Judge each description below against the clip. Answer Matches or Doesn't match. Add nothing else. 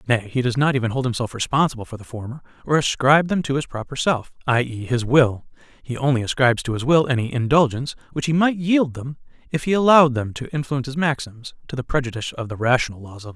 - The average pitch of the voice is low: Matches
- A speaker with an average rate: Doesn't match